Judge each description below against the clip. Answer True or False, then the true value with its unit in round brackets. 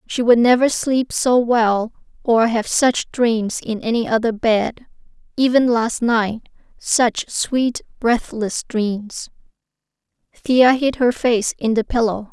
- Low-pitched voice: False (235 Hz)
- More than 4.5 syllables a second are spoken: False (3.5 syllables/s)